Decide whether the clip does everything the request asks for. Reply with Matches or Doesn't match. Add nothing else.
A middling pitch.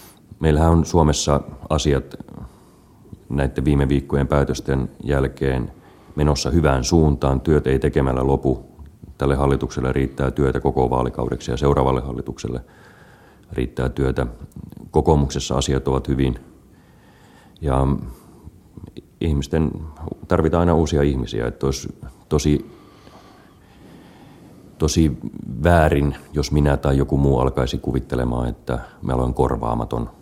Doesn't match